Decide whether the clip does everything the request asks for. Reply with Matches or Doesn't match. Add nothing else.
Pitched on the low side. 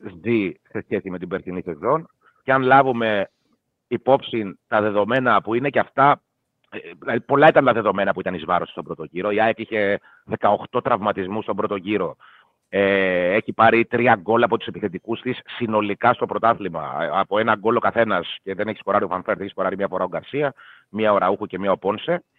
Matches